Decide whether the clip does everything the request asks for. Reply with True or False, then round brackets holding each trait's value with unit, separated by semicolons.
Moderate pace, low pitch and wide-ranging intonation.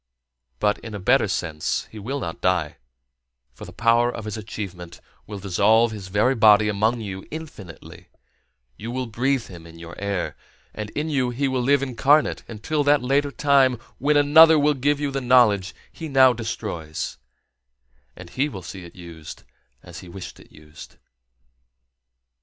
True (165 wpm; 110 Hz; 6.3 semitones)